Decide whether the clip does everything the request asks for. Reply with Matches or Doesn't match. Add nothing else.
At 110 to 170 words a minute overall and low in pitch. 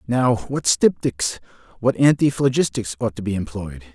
Matches